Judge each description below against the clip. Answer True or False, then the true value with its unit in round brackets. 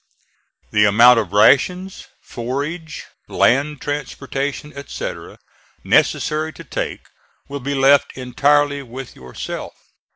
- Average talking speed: False (100 wpm)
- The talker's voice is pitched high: False (140 Hz)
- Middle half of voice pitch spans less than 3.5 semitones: True (2.9 semitones)